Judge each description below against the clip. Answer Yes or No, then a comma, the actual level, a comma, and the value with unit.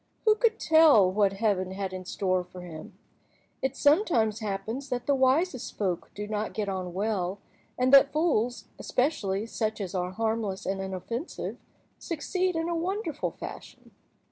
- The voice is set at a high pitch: Yes, high, 220 Hz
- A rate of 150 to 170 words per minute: Yes, average, 155 wpm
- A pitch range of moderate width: No, wide, 7.0 semitones